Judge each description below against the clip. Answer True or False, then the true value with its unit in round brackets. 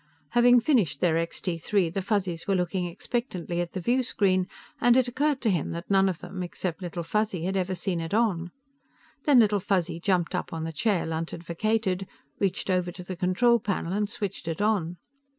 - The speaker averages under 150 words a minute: False (200 wpm)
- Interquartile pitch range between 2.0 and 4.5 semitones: True (3.6 semitones)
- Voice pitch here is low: False (185 Hz)